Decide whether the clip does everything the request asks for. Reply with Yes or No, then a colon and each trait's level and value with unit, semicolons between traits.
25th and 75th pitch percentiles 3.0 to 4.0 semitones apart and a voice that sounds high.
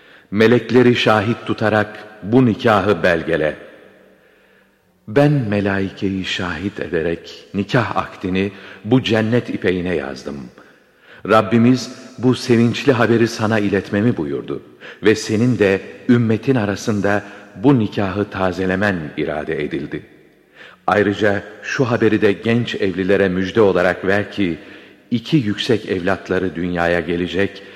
No: average, 3.3 semitones; low, 105 Hz